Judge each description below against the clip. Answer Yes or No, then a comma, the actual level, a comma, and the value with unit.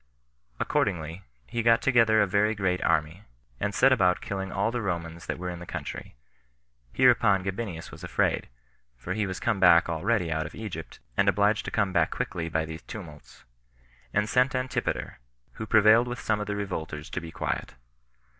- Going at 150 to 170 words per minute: No, average, 180 wpm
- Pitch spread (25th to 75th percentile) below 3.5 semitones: No, average, 4.6 semitones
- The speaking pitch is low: Yes, very low, 95 Hz